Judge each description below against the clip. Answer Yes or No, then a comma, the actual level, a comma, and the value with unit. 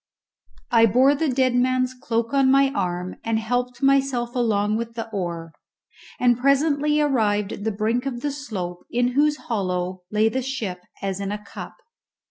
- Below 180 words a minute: Yes, average, 170 wpm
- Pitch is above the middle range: Yes, high, 240 Hz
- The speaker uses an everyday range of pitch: Yes, average, 4.4 semitones